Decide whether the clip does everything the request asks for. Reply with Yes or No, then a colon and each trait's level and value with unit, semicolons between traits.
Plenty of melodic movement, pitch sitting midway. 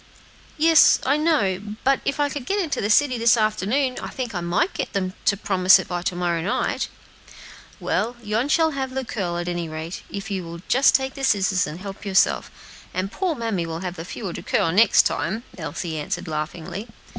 No: wide, 6.7 semitones; high, 200 Hz